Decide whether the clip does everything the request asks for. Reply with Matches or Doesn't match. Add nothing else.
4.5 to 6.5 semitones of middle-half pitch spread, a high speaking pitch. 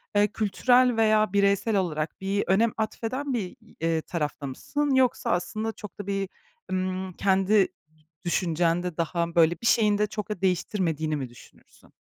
Doesn't match